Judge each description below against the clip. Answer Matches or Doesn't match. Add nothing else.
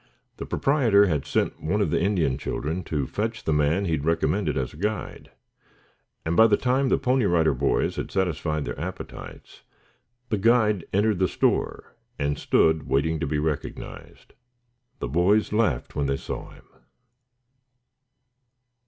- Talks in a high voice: Doesn't match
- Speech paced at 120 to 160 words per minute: Matches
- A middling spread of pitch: Doesn't match